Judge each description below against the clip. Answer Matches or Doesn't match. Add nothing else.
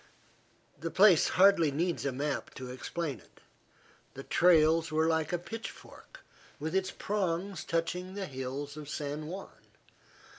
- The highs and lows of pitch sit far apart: Doesn't match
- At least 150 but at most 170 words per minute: Doesn't match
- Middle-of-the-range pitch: Matches